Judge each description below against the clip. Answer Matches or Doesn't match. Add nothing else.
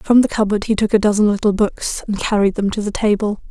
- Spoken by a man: Doesn't match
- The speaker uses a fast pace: Matches